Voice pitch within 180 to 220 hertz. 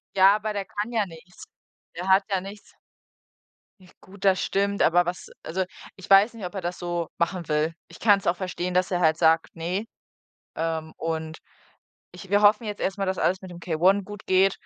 Yes: medium, 185 Hz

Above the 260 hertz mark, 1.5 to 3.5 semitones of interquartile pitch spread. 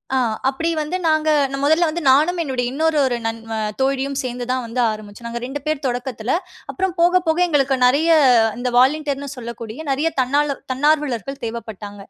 No: very high, 270 Hz; average, 4.0 semitones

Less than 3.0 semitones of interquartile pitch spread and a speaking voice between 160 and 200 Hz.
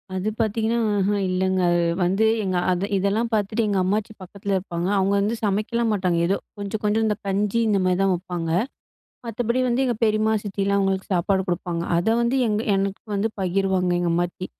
Yes: narrow, 2.6 semitones; high, 195 Hz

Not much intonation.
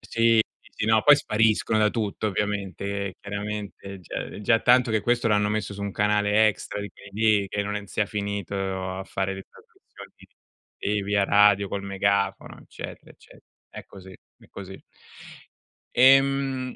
Yes: narrow, 1.8 semitones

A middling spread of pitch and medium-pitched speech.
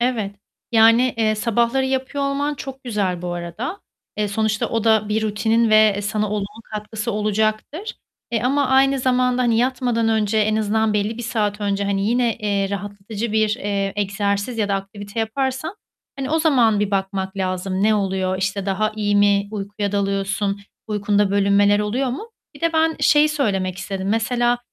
No: average, 3.1 semitones; high, 215 Hz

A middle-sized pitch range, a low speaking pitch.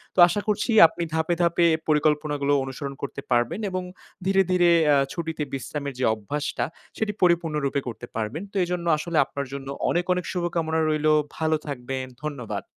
No: average, 3.6 semitones; medium, 155 Hz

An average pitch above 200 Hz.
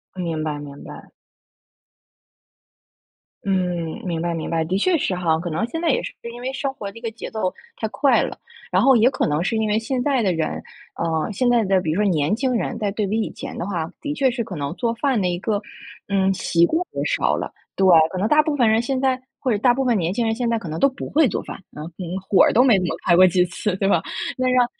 Yes: high, 210 Hz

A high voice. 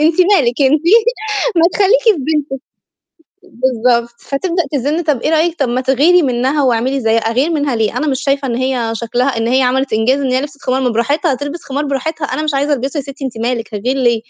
Yes: very high, 270 Hz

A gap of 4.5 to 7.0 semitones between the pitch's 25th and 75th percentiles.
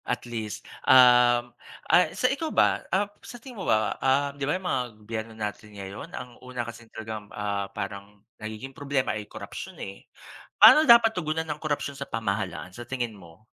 Yes: average, 5.1 semitones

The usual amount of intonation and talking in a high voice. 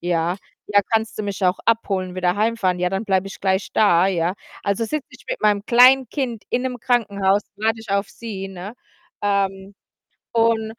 Yes: average, 3.0 semitones; high, 205 Hz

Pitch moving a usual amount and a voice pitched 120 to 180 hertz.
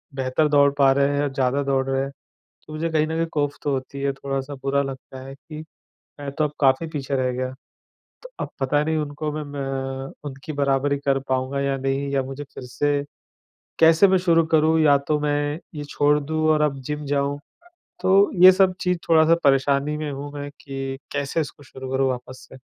No: narrow, 2.0 semitones; medium, 140 Hz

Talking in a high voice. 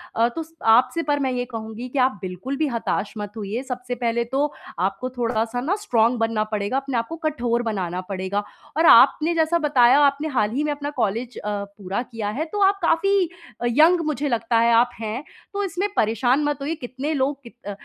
Yes: very high, 250 Hz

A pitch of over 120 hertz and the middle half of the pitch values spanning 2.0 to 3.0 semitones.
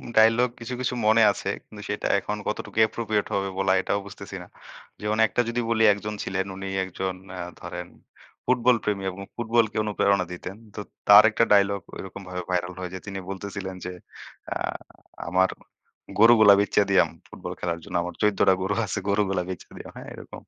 No: low, 100 Hz; narrow, 2.4 semitones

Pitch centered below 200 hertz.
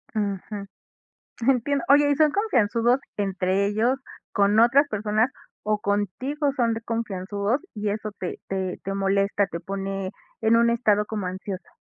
No: high, 210 Hz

